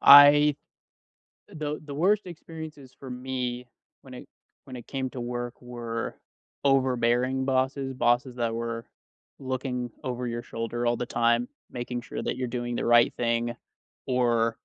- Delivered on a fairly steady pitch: Yes, narrow, 1.9 semitones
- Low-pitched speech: Yes, low, 125 Hz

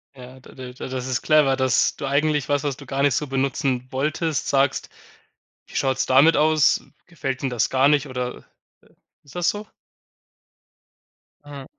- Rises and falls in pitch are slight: Yes, narrow, 2.2 semitones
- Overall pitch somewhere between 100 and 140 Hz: Yes, low, 135 Hz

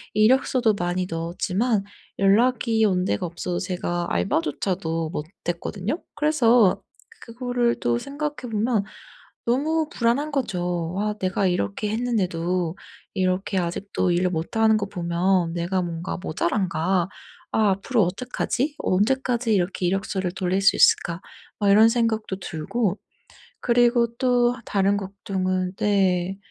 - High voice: Yes, high, 195 Hz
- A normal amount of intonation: Yes, average, 4.8 semitones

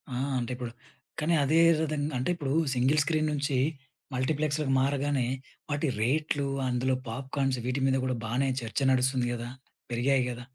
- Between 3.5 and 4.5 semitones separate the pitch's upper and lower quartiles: No, narrow, 2.5 semitones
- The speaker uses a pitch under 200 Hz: Yes, low, 135 Hz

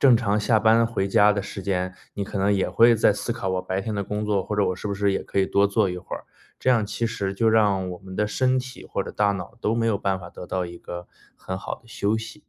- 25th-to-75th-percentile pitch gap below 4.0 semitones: Yes, average, 2.7 semitones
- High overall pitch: No, low, 100 Hz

